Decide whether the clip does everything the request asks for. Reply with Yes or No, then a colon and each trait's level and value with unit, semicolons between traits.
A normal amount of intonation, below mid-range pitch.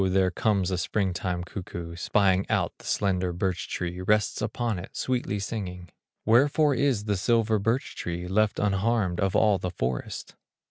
Yes: average, 3.3 semitones; very low, 95 Hz